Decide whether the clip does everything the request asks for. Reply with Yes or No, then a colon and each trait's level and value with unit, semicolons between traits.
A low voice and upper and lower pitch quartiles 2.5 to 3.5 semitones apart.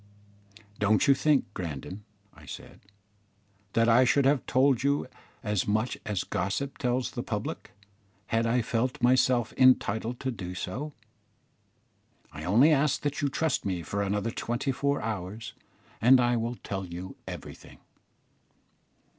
No: low, 120 Hz; average, 4.4 semitones